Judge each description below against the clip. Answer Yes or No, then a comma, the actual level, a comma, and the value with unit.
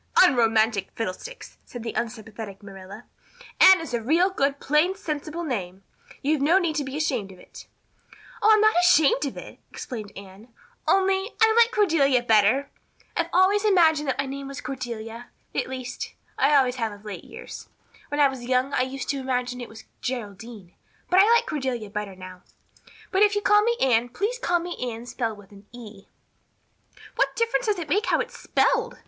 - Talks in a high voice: Yes, very high, 265 Hz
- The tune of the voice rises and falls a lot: Yes, wide, 7.4 semitones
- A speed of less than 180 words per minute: No, average, 185 wpm